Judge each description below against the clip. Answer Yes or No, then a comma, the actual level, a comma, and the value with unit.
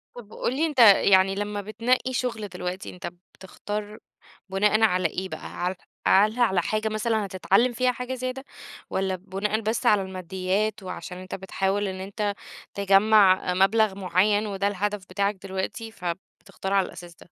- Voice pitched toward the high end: Yes, high, 200 Hz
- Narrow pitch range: Yes, narrow, 2.3 semitones